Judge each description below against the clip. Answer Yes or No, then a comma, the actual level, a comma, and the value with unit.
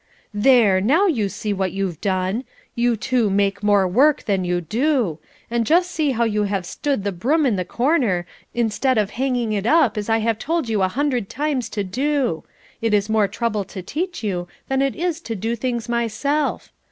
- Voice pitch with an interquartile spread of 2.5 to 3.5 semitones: No, average, 5.1 semitones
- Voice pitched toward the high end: Yes, high, 225 Hz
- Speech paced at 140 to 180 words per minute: No, average, 200 wpm